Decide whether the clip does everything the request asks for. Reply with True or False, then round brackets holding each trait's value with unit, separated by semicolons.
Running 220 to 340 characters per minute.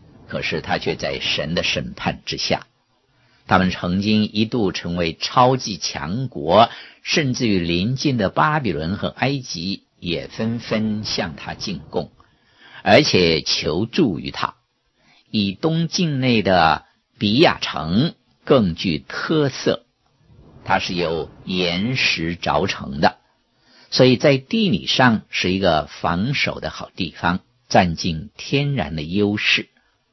False (180 characters per minute)